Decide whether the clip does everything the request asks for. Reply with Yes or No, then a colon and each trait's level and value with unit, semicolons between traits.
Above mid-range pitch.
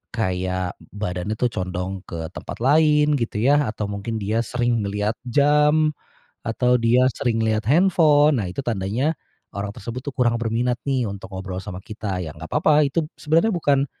No: low, 115 Hz